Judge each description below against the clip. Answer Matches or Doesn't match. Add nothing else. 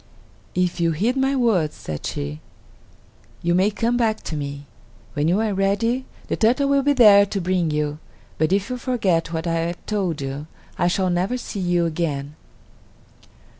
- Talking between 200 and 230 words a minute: Doesn't match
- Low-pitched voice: Doesn't match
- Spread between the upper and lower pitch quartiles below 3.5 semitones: Doesn't match